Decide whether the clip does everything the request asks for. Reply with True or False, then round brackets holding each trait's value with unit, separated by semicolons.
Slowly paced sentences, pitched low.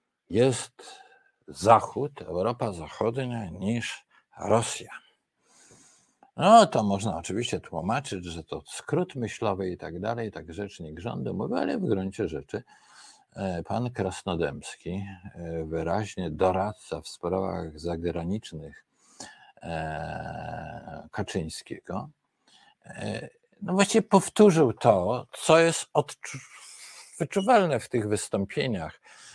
True (90 wpm; 105 Hz)